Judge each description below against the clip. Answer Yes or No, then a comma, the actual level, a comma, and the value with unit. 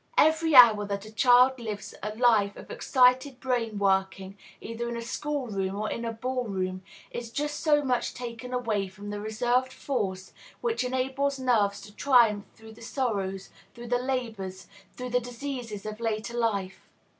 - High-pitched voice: Yes, high, 235 Hz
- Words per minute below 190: Yes, average, 170 wpm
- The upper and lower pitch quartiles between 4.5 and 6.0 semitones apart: No, average, 3.6 semitones